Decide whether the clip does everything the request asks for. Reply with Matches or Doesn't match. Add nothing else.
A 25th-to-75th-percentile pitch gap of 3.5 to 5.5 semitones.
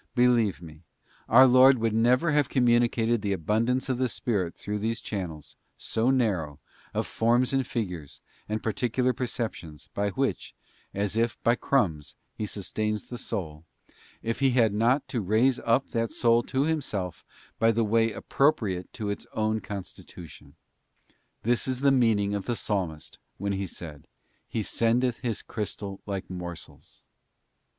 Matches